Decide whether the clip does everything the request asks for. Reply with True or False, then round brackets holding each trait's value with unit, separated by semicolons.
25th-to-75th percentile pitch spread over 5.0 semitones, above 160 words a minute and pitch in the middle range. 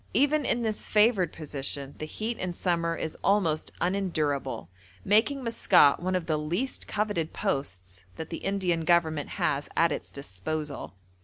False (5.5 semitones; 150 wpm; 165 Hz)